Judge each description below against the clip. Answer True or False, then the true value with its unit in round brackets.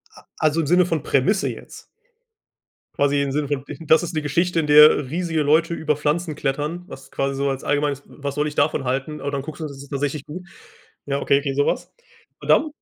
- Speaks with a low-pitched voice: False (150 Hz)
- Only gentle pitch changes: True (2.1 semitones)